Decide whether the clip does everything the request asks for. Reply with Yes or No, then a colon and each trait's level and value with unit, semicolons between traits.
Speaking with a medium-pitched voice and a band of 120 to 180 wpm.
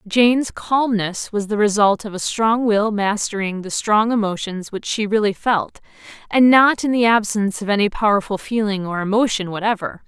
No: high, 210 Hz; average, 175 wpm